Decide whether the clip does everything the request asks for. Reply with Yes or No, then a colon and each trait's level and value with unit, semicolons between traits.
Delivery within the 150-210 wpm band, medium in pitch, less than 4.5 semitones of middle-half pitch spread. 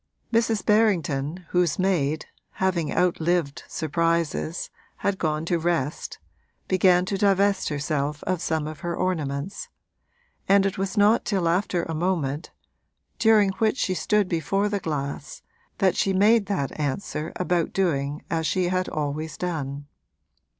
No: slow, 135 wpm; medium, 175 Hz; average, 4.0 semitones